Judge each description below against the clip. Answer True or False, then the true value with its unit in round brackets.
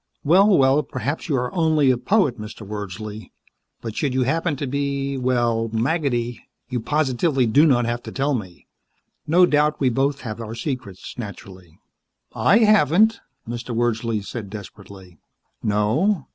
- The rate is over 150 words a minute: True (160 wpm)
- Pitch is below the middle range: True (125 Hz)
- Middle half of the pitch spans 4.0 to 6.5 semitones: True (4.7 semitones)